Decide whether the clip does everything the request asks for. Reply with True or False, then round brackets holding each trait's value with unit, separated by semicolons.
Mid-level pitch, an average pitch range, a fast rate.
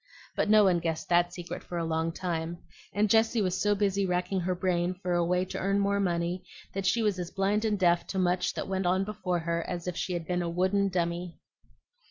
False (180 Hz; 2.2 semitones; 235 wpm)